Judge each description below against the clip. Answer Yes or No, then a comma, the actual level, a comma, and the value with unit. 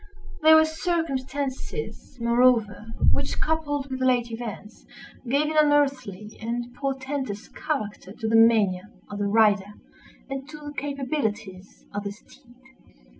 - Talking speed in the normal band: No, slow, 125 wpm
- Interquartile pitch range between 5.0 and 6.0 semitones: Yes, wide, 5.4 semitones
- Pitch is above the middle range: Yes, very high, 250 Hz